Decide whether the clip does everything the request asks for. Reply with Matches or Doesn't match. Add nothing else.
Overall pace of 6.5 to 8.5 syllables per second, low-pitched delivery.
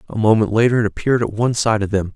Matches